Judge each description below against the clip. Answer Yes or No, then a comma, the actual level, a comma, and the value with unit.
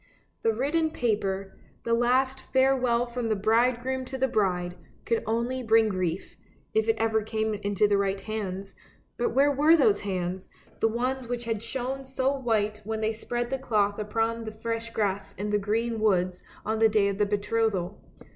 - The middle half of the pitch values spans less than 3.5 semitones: Yes, average, 3.1 semitones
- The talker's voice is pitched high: Yes, high, 225 Hz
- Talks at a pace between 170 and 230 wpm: Yes, average, 180 wpm